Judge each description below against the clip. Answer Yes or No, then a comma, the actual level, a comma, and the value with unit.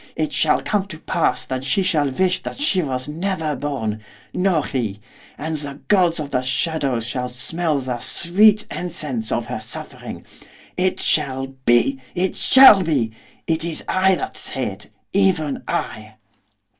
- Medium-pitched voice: Yes, medium, 155 Hz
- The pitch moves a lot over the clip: Yes, wide, 5.8 semitones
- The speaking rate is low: No, average, 155 wpm